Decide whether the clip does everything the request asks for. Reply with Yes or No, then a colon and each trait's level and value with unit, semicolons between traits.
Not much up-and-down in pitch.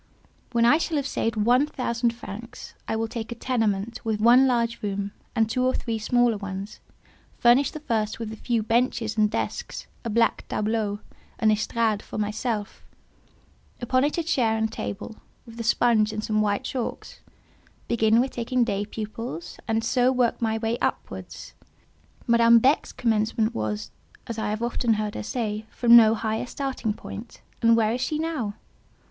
Yes: narrow, 2.1 semitones